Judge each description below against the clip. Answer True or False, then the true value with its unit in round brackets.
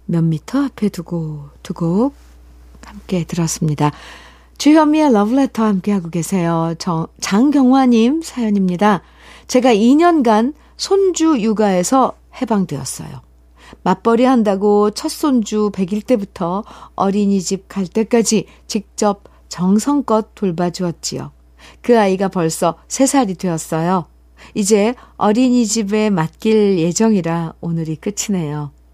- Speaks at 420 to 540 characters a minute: False (250 characters per minute)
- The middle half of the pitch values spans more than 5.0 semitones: True (5.4 semitones)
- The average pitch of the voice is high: True (200 Hz)